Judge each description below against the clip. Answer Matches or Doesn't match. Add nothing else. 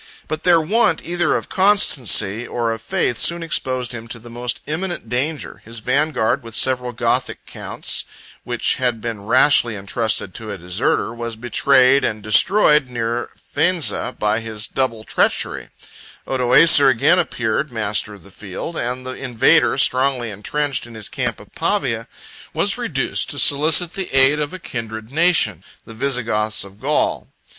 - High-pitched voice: Doesn't match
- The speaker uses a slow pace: Doesn't match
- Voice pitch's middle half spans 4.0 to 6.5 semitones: Matches